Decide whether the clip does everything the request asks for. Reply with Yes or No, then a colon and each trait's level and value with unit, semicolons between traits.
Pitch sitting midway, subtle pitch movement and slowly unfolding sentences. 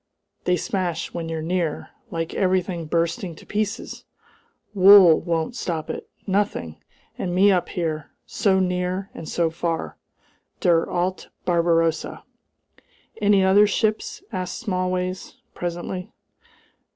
Yes: medium, 180 Hz; narrow, 2.3 semitones; slow, 115 wpm